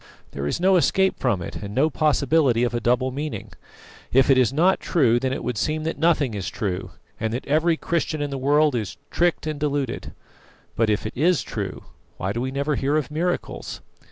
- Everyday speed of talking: No, fast, 210 wpm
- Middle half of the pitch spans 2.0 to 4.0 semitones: No, average, 4.5 semitones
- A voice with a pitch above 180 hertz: No, medium, 140 Hz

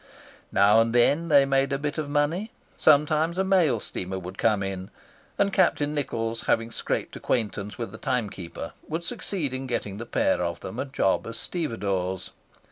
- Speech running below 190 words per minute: Yes, average, 175 wpm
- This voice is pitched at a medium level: No, low, 125 Hz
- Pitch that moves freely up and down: Yes, wide, 6.5 semitones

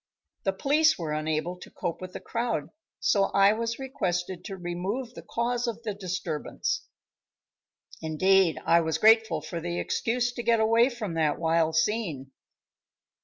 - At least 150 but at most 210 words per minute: Yes, average, 155 wpm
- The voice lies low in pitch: No, high, 190 Hz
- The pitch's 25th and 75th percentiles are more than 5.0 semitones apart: Yes, wide, 5.6 semitones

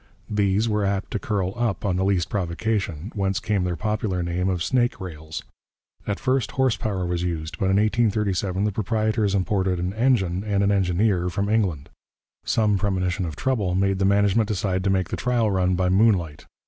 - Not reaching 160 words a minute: No, average, 185 wpm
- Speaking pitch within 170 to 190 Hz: No, low, 100 Hz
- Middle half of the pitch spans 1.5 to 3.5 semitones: Yes, average, 2.8 semitones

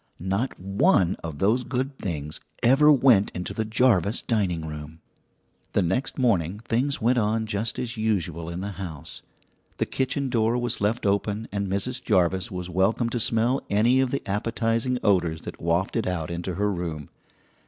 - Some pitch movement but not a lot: Yes, average, 5.0 semitones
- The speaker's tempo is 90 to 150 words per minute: No, average, 165 wpm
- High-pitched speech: No, low, 105 Hz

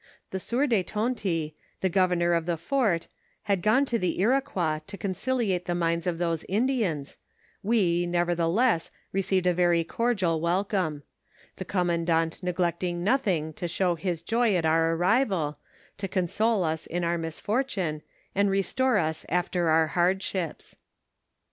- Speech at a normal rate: Yes, average, 145 wpm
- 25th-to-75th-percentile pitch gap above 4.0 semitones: No, average, 3.4 semitones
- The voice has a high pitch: No, medium, 180 Hz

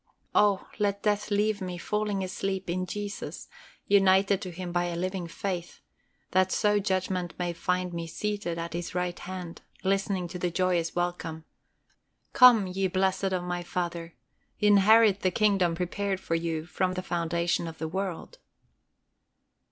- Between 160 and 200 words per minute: No, average, 150 wpm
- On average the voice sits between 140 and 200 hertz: Yes, medium, 185 Hz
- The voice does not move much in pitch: Yes, narrow, 2.2 semitones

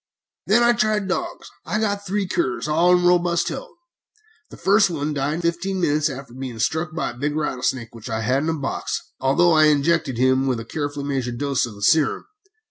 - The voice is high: No, medium, 150 Hz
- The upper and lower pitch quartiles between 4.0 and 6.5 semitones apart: Yes, average, 5.1 semitones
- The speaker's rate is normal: No, fast, 210 wpm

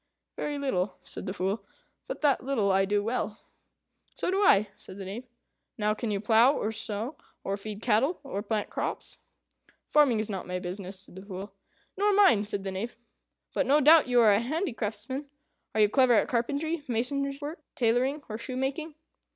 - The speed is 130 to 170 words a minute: No, average, 185 wpm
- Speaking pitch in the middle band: No, high, 230 Hz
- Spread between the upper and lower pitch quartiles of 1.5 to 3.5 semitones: No, wide, 5.5 semitones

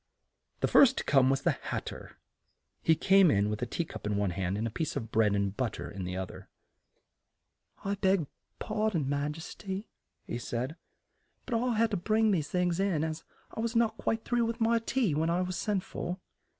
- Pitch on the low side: No, medium, 170 Hz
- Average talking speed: No, fast, 220 wpm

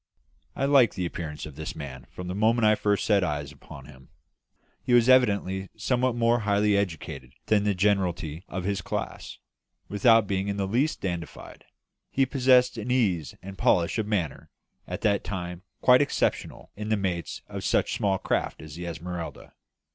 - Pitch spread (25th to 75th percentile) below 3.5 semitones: No, average, 4.3 semitones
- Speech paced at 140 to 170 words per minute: No, average, 180 wpm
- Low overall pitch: Yes, low, 100 Hz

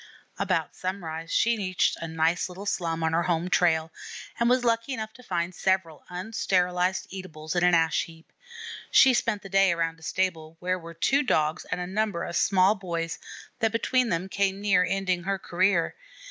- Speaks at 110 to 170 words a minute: No, average, 185 wpm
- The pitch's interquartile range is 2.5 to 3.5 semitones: Yes, average, 2.9 semitones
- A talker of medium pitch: Yes, medium, 180 Hz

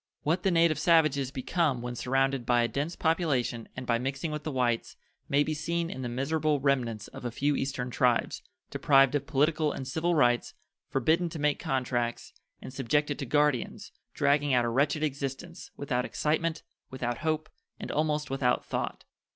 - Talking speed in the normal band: Yes, average, 175 wpm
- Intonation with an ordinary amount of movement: Yes, average, 3.5 semitones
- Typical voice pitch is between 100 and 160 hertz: Yes, medium, 140 Hz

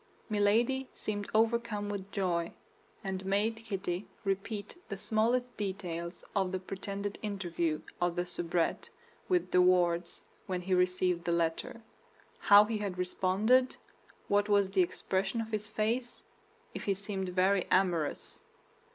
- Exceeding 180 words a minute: No, slow, 135 wpm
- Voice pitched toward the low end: No, high, 195 Hz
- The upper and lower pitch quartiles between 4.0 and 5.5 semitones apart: No, average, 2.8 semitones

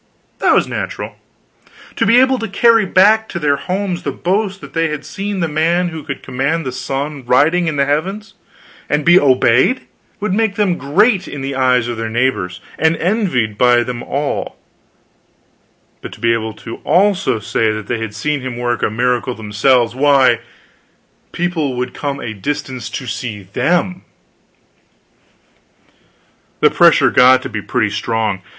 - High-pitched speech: No, medium, 140 Hz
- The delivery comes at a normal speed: Yes, average, 165 wpm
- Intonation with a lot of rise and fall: Yes, wide, 6.7 semitones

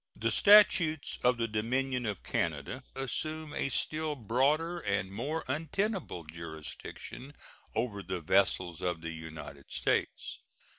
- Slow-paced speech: Yes, slow, 120 wpm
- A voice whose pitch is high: No, low, 120 Hz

